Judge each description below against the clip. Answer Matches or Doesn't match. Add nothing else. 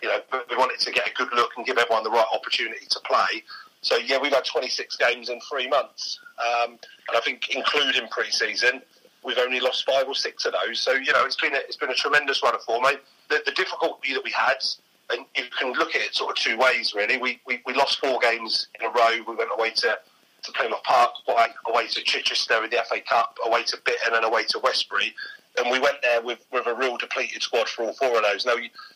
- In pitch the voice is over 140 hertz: Doesn't match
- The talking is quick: Matches